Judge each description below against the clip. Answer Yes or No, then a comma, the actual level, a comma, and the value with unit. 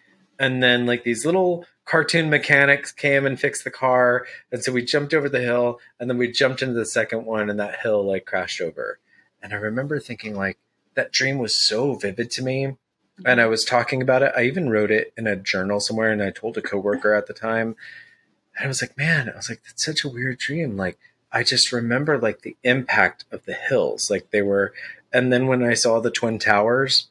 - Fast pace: Yes, fast, 225 wpm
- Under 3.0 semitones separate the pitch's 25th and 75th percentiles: No, average, 3.7 semitones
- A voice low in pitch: Yes, low, 125 Hz